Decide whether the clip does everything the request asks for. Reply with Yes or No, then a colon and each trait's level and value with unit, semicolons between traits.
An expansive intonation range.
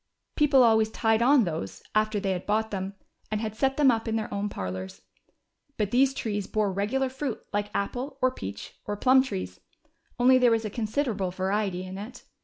No: average, 4.2 semitones